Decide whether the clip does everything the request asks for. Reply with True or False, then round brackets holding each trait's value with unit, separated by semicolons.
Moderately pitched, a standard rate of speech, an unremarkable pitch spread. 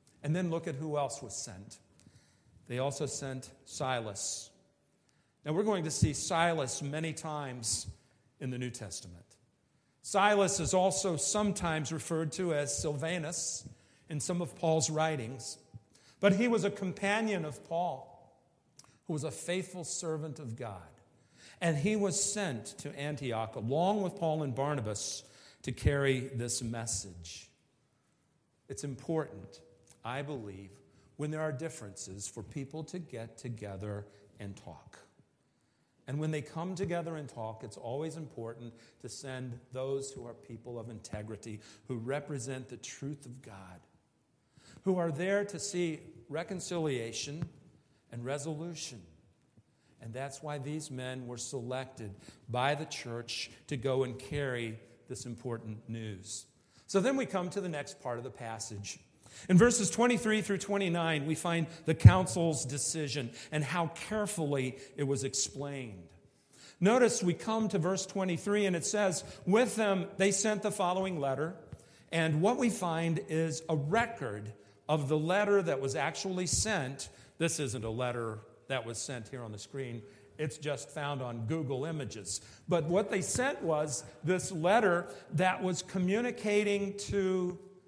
False (145 Hz; 145 wpm; 6.4 semitones)